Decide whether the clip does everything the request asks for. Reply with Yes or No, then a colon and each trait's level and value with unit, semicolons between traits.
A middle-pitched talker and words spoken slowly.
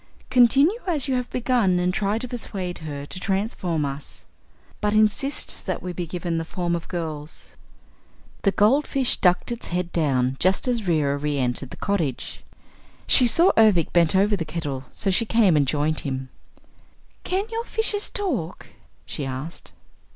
No: medium, 180 Hz; average, 165 wpm